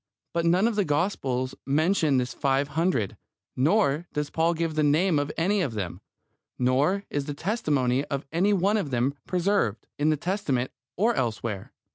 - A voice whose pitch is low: No, medium, 150 Hz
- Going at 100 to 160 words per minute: No, average, 175 wpm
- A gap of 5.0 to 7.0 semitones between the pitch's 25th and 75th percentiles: Yes, wide, 5.6 semitones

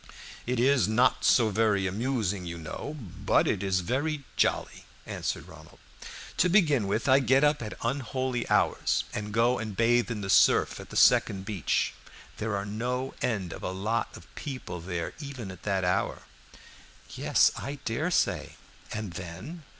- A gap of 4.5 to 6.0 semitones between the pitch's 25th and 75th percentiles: Yes, average, 5.2 semitones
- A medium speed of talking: Yes, average, 170 wpm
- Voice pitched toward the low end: Yes, low, 115 Hz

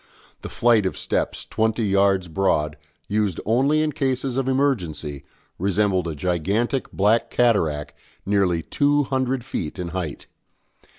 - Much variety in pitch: Yes, wide, 6.4 semitones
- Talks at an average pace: No, slow, 130 wpm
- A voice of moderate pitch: No, low, 105 Hz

